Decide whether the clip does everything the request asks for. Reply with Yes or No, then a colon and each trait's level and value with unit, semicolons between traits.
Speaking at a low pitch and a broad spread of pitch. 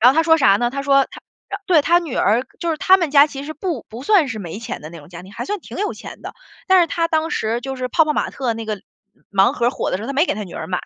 No: very high, 275 Hz; wide, 6.7 semitones